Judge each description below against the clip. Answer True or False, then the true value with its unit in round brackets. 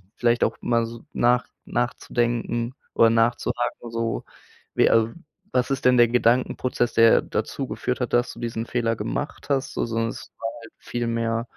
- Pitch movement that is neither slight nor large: False (1.1 semitones)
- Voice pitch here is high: False (120 Hz)